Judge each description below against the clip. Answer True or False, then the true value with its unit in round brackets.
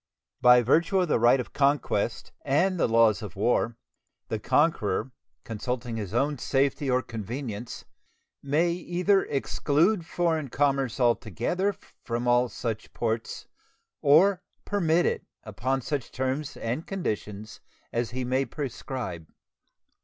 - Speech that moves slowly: True (125 wpm)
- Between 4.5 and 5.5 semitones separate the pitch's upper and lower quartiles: True (4.9 semitones)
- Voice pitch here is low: True (130 Hz)